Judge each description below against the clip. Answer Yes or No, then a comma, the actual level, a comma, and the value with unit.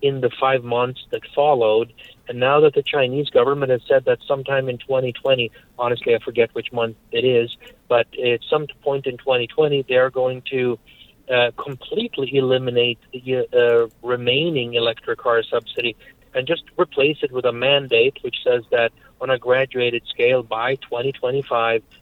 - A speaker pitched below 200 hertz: Yes, low, 135 Hz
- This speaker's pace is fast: No, average, 165 wpm